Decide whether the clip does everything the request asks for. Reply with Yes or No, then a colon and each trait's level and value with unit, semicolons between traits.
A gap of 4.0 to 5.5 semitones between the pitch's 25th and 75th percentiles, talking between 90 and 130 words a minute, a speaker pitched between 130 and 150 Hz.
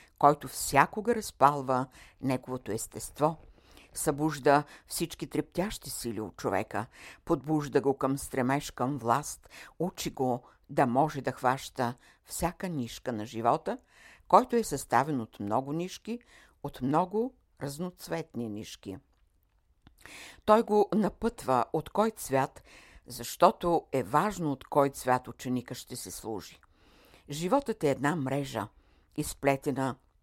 Yes: average, 5.2 semitones; slow, 115 wpm; medium, 140 Hz